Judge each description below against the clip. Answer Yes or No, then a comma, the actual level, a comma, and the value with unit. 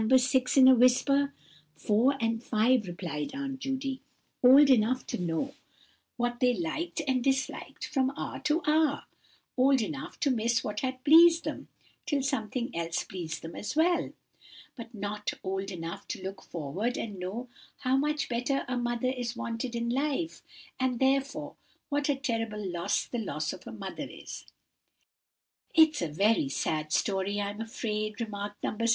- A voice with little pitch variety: No, average, 4.7 semitones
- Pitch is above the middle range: Yes, high, 240 Hz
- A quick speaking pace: No, average, 160 wpm